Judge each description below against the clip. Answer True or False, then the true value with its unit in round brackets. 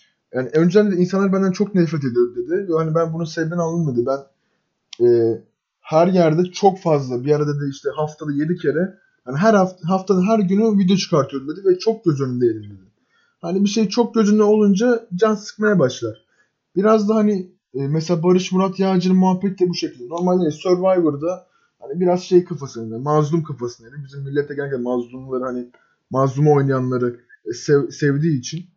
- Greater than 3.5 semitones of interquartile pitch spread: True (5.5 semitones)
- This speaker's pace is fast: True (170 wpm)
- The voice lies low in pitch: False (170 Hz)